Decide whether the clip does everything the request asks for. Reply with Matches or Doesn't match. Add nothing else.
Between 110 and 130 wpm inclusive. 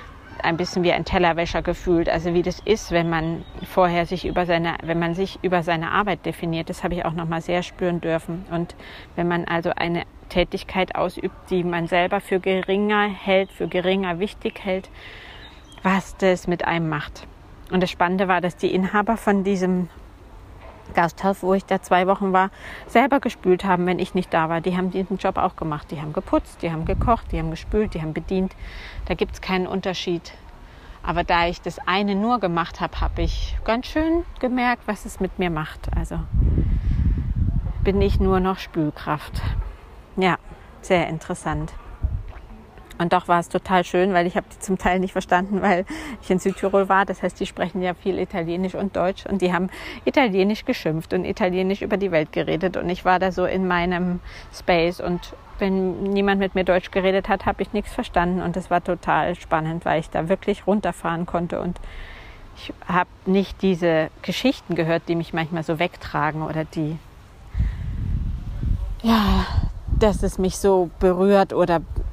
Doesn't match